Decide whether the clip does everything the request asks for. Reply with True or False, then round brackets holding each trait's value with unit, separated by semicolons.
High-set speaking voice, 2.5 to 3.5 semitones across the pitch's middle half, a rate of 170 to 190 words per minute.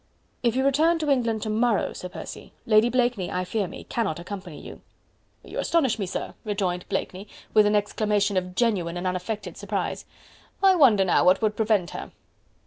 False (210 Hz; 4.3 semitones; 180 wpm)